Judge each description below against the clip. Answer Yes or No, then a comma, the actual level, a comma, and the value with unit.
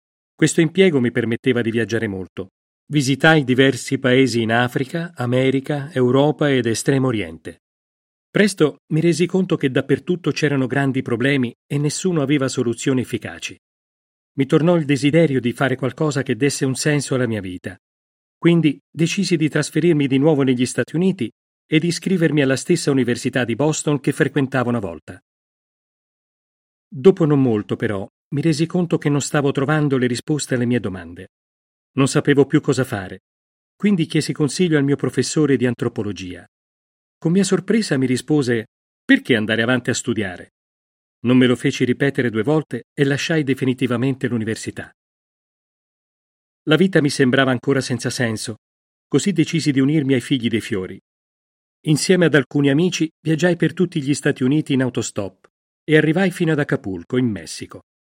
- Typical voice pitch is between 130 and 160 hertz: Yes, low, 135 Hz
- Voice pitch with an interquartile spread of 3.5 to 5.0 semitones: Yes, average, 4.3 semitones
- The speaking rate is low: No, average, 155 wpm